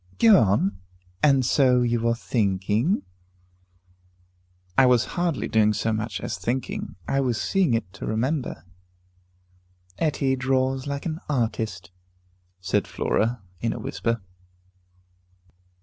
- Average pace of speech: No, slow, 120 wpm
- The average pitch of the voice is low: Yes, low, 120 Hz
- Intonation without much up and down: No, average, 3.9 semitones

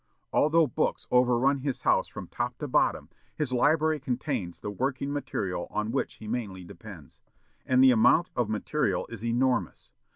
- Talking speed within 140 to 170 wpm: Yes, average, 160 wpm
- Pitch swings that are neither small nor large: Yes, average, 4.5 semitones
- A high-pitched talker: No, low, 125 Hz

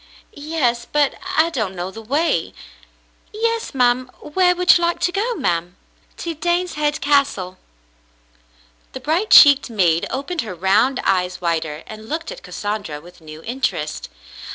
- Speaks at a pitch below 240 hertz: No, very high, 255 Hz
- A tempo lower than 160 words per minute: Yes, average, 145 wpm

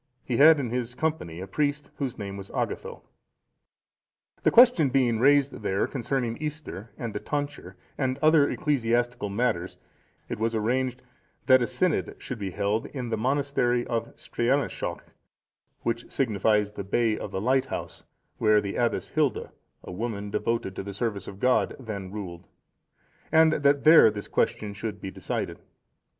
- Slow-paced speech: No, average, 155 wpm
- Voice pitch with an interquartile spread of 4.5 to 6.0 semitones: Yes, average, 4.8 semitones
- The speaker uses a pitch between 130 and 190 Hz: No, low, 120 Hz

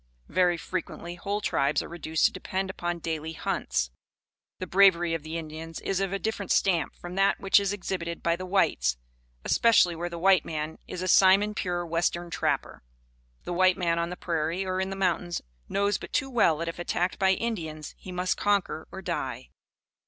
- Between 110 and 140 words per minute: No, average, 190 wpm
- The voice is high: No, medium, 175 Hz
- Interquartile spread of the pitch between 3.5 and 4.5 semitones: No, narrow, 2.5 semitones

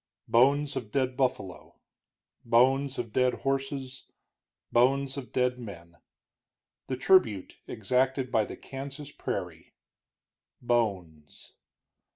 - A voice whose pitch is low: Yes, low, 125 Hz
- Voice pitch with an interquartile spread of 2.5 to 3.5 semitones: Yes, average, 2.9 semitones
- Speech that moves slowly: Yes, slow, 100 wpm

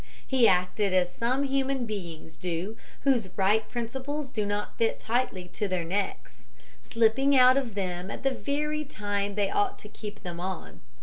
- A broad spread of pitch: Yes, wide, 5.8 semitones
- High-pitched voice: Yes, high, 215 Hz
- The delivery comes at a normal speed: Yes, average, 170 wpm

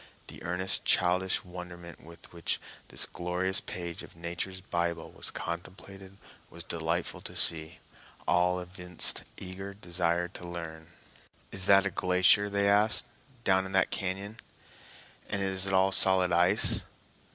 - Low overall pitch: Yes, very low, 90 Hz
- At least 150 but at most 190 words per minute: No, average, 140 wpm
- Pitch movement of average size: No, narrow, 1.8 semitones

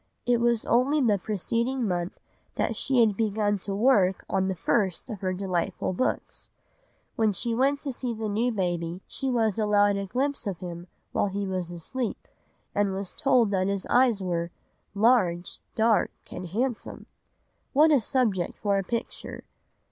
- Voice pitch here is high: Yes, high, 205 Hz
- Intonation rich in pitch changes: No, average, 4.2 semitones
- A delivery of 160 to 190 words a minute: Yes, average, 165 wpm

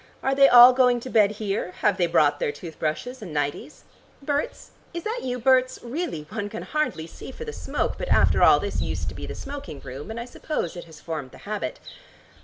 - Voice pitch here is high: Yes, high, 225 Hz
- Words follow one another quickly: Yes, fast, 220 wpm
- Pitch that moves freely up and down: Yes, wide, 8.2 semitones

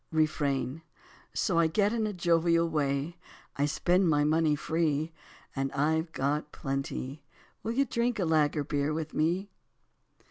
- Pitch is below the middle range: No, medium, 160 Hz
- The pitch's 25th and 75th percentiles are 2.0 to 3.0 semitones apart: Yes, average, 2.7 semitones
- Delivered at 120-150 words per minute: Yes, average, 140 wpm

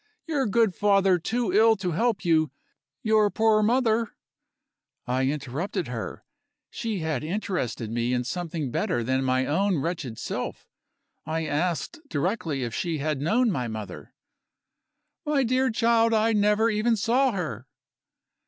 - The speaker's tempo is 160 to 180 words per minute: No, average, 145 wpm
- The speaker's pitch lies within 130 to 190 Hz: Yes, medium, 185 Hz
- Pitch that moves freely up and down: Yes, wide, 8.0 semitones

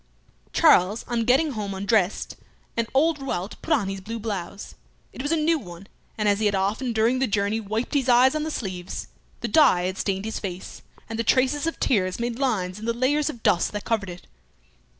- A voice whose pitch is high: Yes, high, 225 Hz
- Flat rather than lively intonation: No, average, 5.0 semitones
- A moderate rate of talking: No, fast, 210 wpm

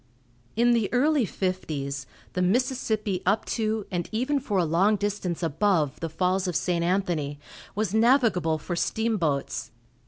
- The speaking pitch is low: No, high, 190 Hz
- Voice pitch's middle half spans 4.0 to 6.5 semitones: Yes, average, 4.6 semitones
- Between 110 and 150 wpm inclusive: Yes, average, 145 wpm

